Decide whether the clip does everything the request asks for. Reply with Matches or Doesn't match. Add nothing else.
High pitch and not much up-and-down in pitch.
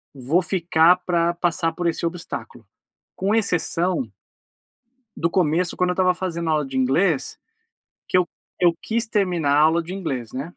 Doesn't match